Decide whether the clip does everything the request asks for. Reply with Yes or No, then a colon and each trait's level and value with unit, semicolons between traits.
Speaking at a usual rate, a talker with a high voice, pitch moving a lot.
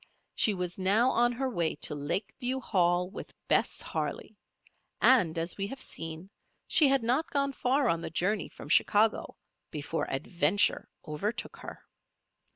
Yes: average, 150 wpm; high, 200 Hz; wide, 6.7 semitones